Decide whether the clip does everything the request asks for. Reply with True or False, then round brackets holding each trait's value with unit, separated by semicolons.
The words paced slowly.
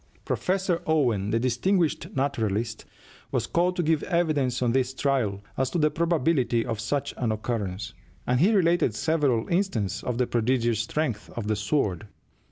False (160 wpm)